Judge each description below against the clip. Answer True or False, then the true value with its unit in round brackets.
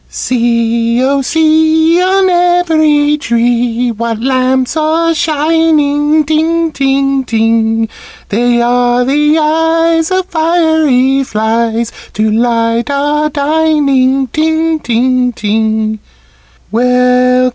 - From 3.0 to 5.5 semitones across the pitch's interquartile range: True (5.0 semitones)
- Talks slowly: True (90 wpm)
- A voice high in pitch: True (275 Hz)